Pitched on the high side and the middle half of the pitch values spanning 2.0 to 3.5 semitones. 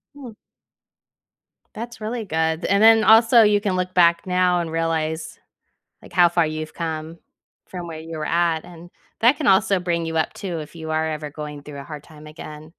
No: medium, 170 Hz; average, 3.2 semitones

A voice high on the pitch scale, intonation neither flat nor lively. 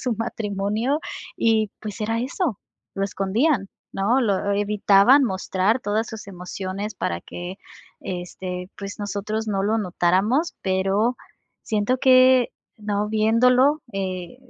Yes: high, 210 Hz; average, 3.0 semitones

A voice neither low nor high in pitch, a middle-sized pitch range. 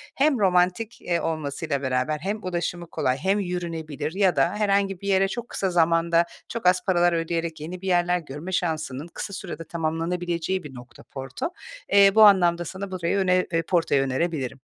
Yes: medium, 175 Hz; average, 3.0 semitones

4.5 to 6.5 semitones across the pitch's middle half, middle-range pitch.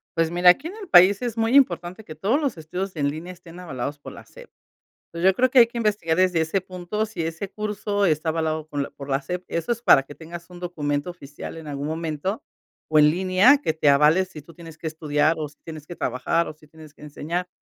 No: average, 3.7 semitones; medium, 170 Hz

